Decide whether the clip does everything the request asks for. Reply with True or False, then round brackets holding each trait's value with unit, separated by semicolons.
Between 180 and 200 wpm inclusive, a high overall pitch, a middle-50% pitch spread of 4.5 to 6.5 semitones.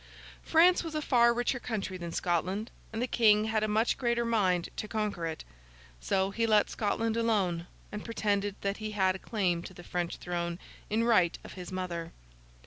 False (190 wpm; 210 Hz; 4.0 semitones)